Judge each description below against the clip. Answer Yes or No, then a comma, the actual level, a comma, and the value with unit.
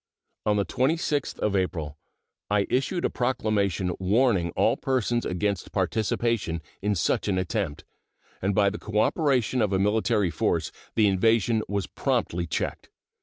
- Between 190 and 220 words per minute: No, average, 140 wpm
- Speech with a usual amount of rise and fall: Yes, average, 3.8 semitones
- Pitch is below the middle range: Yes, low, 105 Hz